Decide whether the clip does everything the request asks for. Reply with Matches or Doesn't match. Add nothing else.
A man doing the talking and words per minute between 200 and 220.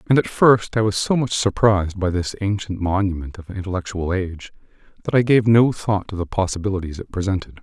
Matches